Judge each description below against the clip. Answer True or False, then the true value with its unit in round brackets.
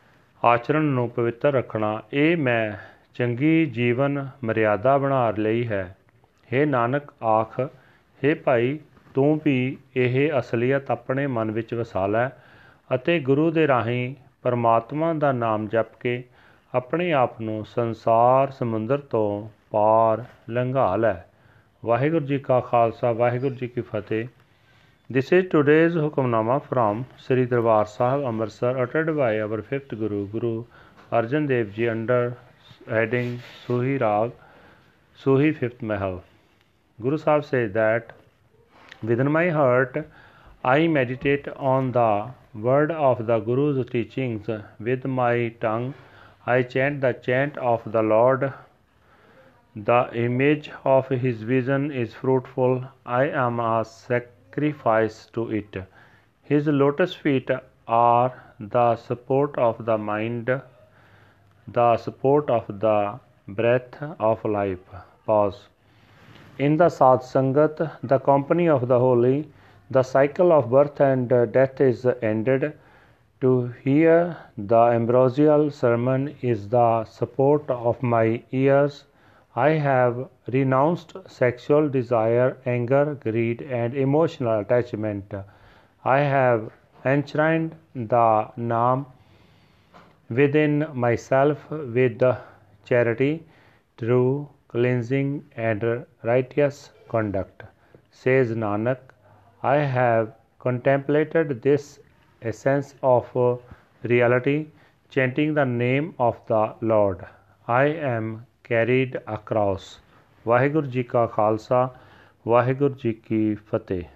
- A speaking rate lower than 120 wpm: True (110 wpm)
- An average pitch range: True (3.4 semitones)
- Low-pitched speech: True (125 Hz)